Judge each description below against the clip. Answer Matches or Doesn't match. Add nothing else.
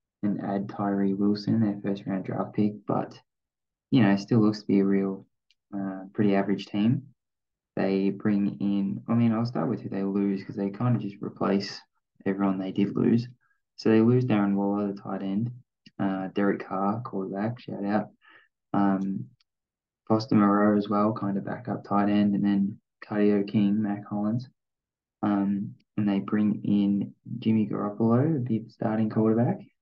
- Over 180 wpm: Doesn't match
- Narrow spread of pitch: Matches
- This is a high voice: Doesn't match